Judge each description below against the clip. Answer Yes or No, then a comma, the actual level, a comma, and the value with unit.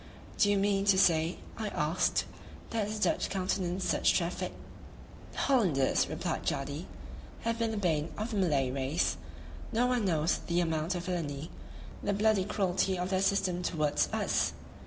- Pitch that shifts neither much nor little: Yes, average, 4.2 semitones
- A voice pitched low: No, medium, 185 Hz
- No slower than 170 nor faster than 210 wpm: No, average, 160 wpm